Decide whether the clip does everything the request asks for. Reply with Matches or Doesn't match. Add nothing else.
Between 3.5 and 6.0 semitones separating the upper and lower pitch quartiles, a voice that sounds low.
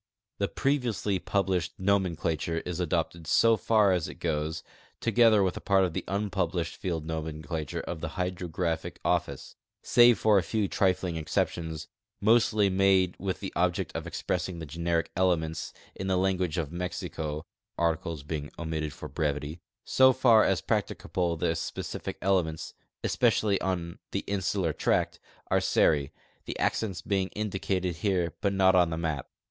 Doesn't match